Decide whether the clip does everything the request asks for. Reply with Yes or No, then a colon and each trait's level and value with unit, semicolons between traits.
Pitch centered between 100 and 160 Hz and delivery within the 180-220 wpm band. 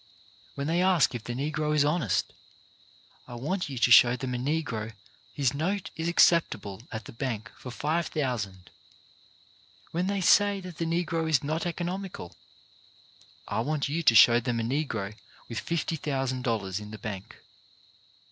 No: medium, 140 Hz; average, 155 wpm